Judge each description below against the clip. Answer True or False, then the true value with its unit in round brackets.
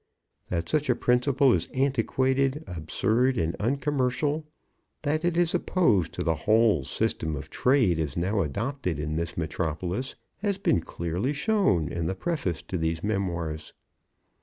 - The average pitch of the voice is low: True (110 Hz)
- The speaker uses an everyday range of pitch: False (8.7 semitones)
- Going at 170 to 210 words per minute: False (145 wpm)